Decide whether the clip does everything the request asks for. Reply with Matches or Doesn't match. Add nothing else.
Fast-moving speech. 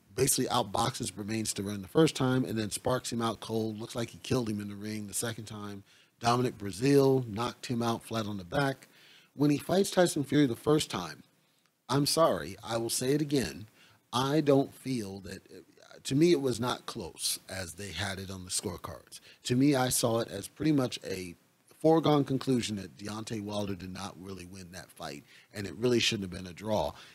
Matches